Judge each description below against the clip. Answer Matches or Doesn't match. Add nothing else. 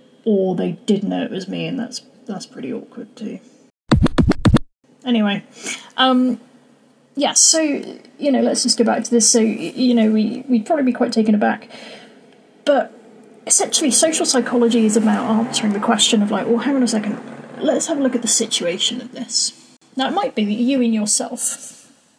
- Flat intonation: Matches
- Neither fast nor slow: Matches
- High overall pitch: Matches